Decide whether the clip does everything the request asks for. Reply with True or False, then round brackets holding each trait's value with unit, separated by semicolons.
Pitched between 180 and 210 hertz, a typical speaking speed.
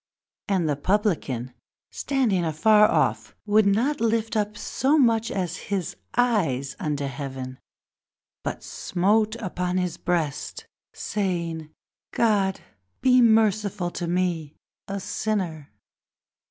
False (190 Hz; 100 wpm)